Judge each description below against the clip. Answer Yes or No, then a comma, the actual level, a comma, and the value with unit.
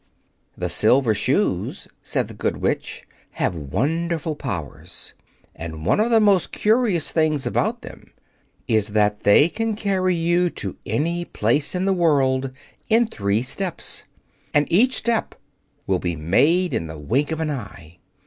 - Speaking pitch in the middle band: Yes, medium, 150 Hz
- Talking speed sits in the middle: Yes, average, 150 wpm